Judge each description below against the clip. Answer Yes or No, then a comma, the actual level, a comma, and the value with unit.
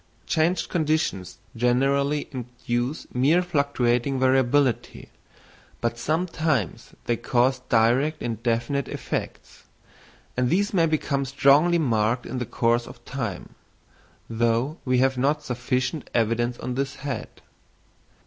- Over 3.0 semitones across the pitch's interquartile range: Yes, average, 3.4 semitones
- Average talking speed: No, slow, 115 wpm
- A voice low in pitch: Yes, low, 130 Hz